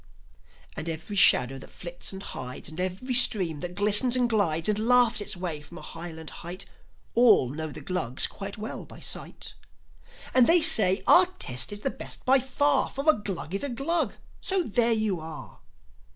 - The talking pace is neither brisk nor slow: Yes, average, 185 wpm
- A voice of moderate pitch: No, high, 200 Hz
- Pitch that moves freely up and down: Yes, wide, 6.9 semitones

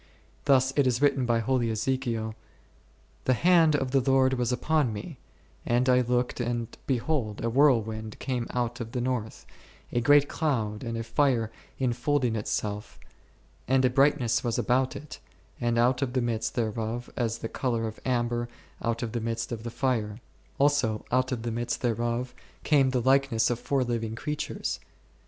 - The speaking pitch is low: Yes, low, 120 Hz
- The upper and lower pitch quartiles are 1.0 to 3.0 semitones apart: Yes, narrow, 2.5 semitones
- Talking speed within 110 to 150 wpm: No, average, 180 wpm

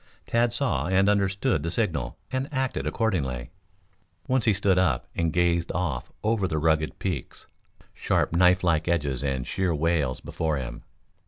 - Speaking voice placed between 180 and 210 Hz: No, very low, 85 Hz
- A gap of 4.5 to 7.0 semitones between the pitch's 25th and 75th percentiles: Yes, average, 4.8 semitones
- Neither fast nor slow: Yes, average, 155 wpm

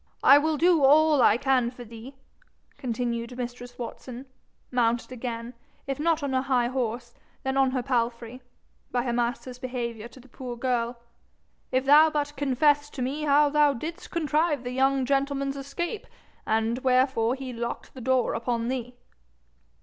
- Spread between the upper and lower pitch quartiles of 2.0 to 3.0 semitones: Yes, average, 2.7 semitones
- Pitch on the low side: No, very high, 255 Hz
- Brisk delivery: No, average, 160 wpm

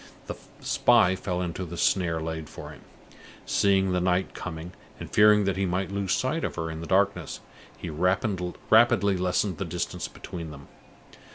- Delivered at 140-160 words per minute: No, average, 170 wpm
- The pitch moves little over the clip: Yes, narrow, 2.3 semitones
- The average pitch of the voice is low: Yes, very low, 90 Hz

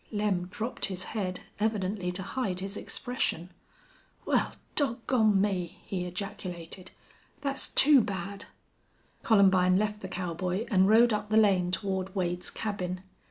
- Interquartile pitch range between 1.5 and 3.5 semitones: Yes, average, 2.8 semitones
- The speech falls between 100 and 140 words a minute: Yes, slow, 135 wpm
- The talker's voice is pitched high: Yes, high, 195 Hz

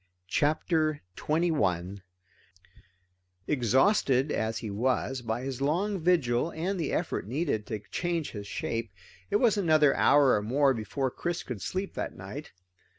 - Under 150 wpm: Yes, average, 140 wpm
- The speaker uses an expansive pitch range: Yes, wide, 6.3 semitones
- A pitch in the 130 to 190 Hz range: Yes, medium, 140 Hz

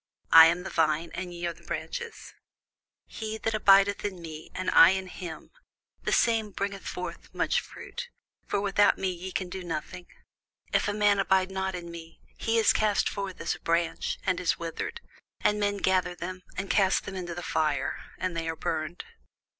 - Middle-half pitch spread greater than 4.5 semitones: No, average, 2.9 semitones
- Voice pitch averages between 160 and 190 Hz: Yes, medium, 185 Hz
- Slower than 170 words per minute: No, average, 185 wpm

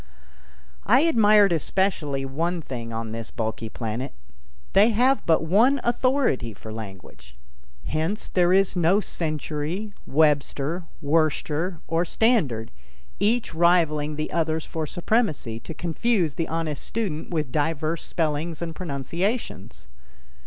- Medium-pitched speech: Yes, medium, 160 Hz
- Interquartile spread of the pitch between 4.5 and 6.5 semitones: Yes, average, 5.1 semitones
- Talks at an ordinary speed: No, slow, 120 wpm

